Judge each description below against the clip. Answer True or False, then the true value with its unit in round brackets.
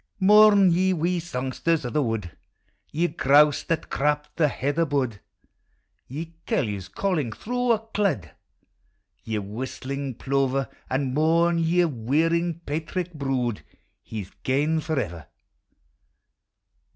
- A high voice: False (150 Hz)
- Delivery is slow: True (115 wpm)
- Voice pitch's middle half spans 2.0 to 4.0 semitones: False (4.5 semitones)